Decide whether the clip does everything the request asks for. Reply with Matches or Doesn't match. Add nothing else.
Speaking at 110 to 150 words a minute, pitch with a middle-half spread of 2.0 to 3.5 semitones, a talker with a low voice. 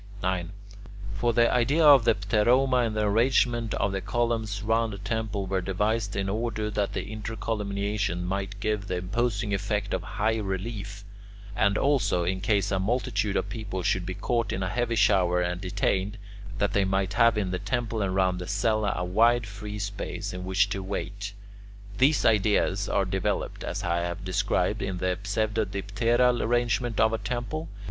Doesn't match